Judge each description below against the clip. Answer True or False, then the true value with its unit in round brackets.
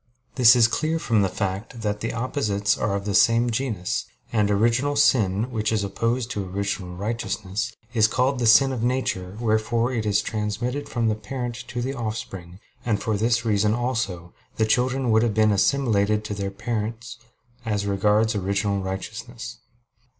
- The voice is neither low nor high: False (110 Hz)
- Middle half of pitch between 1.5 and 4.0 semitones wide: True (3.0 semitones)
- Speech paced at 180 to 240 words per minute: False (165 wpm)